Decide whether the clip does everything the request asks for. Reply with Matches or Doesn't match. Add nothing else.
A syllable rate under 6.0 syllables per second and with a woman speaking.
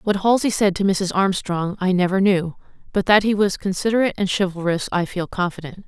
Matches